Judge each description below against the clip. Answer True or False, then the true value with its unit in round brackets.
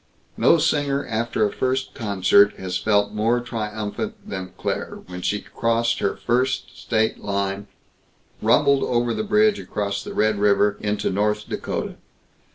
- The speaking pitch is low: True (110 Hz)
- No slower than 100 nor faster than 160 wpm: True (145 wpm)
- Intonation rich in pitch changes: False (3.1 semitones)